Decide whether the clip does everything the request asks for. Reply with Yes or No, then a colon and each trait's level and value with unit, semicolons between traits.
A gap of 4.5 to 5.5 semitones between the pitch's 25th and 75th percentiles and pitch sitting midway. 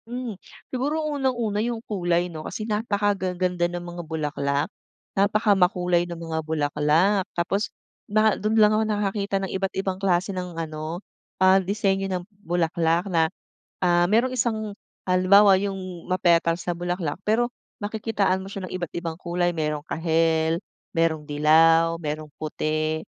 No: average, 3.7 semitones; medium, 180 Hz